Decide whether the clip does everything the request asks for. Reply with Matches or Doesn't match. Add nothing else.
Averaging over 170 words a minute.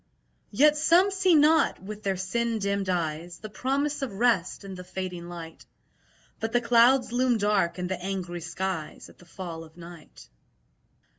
Doesn't match